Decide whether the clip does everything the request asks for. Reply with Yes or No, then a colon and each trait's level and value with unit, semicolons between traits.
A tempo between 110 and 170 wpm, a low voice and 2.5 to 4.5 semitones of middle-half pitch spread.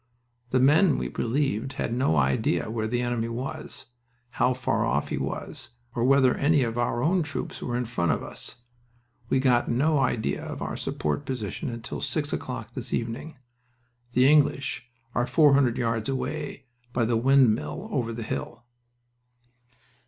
Yes: average, 160 wpm; low, 125 Hz; average, 3.0 semitones